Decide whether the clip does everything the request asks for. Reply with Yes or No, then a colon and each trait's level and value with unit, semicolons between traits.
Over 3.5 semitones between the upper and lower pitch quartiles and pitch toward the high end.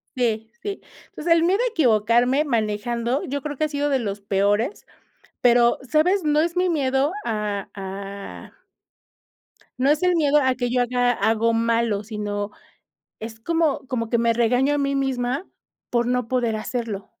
Yes: average, 4.4 semitones; high, 245 Hz